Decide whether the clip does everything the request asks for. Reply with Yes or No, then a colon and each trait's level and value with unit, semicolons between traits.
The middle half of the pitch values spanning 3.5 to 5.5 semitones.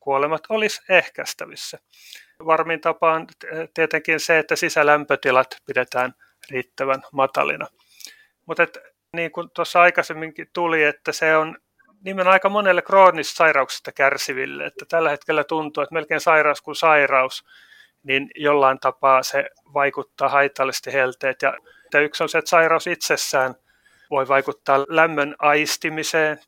No: average, 2.9 semitones